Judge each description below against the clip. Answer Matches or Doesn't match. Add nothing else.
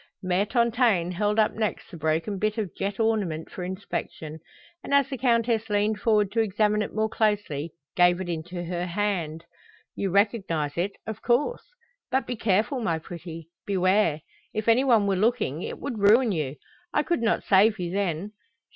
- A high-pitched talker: Matches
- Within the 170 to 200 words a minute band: Matches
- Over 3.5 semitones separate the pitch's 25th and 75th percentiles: Matches